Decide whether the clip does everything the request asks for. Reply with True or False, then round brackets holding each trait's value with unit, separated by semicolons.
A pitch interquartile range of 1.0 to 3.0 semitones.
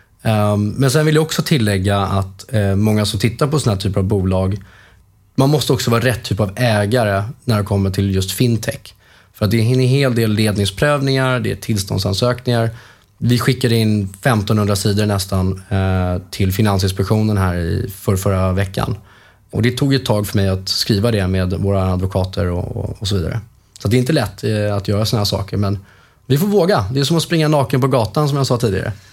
False (3.7 semitones)